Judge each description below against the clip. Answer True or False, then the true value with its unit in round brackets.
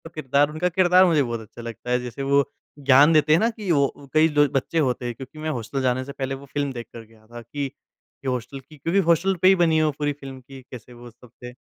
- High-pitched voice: False (140 Hz)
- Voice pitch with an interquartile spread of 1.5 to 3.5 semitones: False (3.9 semitones)